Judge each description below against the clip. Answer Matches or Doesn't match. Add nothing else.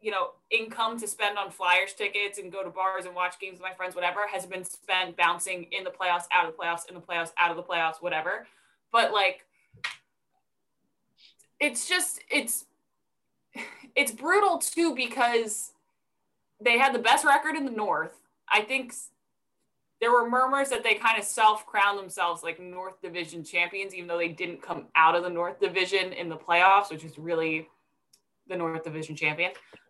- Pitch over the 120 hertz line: Matches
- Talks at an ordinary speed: Matches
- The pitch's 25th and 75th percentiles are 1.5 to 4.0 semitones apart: Doesn't match